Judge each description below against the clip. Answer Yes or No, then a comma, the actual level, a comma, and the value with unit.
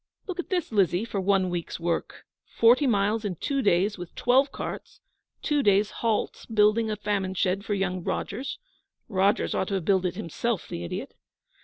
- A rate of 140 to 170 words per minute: No, average, 180 wpm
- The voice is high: Yes, high, 205 Hz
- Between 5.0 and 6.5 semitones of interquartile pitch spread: No, average, 3.5 semitones